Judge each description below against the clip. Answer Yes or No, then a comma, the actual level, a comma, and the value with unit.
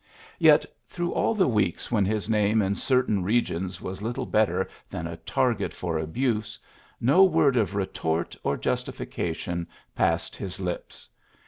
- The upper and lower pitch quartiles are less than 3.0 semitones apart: No, average, 5.2 semitones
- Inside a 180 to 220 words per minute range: No, average, 145 wpm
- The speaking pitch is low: Yes, low, 105 Hz